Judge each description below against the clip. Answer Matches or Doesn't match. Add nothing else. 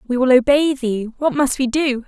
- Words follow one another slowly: Doesn't match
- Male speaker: Doesn't match